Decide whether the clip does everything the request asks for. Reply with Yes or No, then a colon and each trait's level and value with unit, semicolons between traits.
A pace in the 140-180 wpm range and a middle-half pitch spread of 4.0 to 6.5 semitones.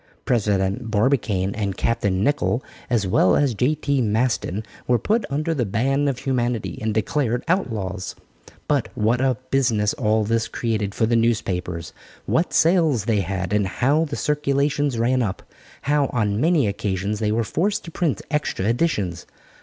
Yes: average, 155 wpm; average, 5.2 semitones